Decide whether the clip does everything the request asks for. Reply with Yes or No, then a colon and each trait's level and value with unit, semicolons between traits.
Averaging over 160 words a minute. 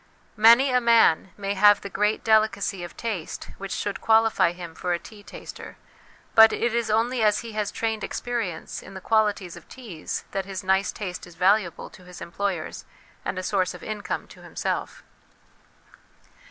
Yes: average, 175 wpm